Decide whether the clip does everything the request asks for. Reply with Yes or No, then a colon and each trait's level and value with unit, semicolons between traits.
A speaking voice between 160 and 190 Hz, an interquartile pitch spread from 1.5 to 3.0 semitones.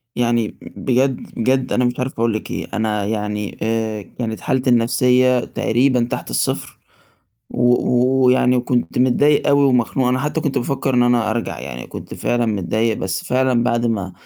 No: low, 120 Hz; narrow, 2.4 semitones